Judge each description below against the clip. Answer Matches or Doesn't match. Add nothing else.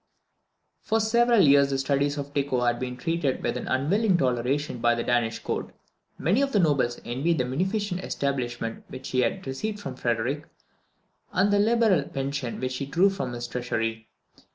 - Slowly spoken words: Doesn't match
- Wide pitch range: Matches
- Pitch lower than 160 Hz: Matches